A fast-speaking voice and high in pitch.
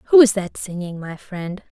No: average, 165 wpm; high, 195 Hz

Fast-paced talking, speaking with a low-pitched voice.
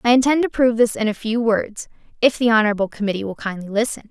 No: fast, 235 wpm; high, 225 Hz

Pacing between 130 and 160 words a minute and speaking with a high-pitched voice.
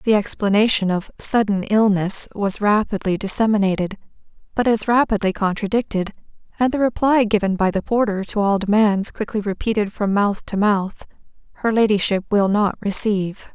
Yes: average, 145 wpm; high, 205 Hz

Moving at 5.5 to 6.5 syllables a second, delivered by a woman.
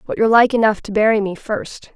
Yes: 6.0 syllables/s; female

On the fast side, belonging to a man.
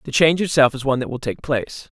Yes: fast, 270 wpm; male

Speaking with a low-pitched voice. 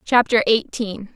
No: high, 215 Hz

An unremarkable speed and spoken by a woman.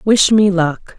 Yes: average, 185 wpm; female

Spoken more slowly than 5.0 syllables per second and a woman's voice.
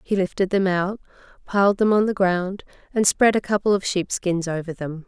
No: 5.2 syllables/s; female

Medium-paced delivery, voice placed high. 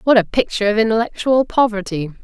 Yes: average, 160 wpm; high, 220 Hz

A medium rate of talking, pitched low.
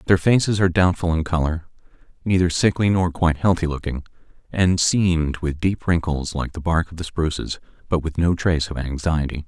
Yes: average, 185 wpm; very low, 85 Hz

